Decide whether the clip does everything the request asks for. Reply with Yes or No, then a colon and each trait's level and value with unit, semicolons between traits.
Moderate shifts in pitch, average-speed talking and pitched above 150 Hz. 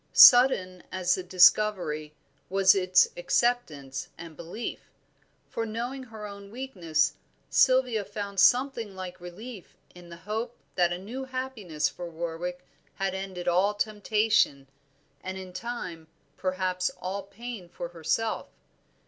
No: average, 4.1 semitones; slow, 125 wpm; high, 190 Hz